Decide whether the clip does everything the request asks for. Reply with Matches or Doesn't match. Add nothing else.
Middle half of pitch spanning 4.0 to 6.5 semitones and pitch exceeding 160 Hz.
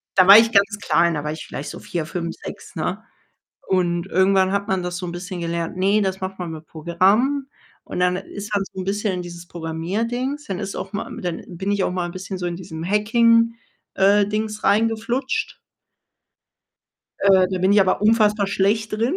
Doesn't match